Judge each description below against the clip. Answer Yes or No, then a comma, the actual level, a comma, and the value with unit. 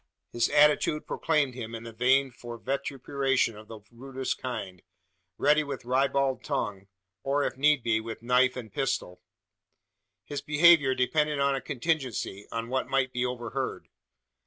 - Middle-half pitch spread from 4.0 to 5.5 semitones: No, average, 3.0 semitones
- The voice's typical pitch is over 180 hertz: No, low, 130 Hz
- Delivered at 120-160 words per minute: Yes, average, 150 wpm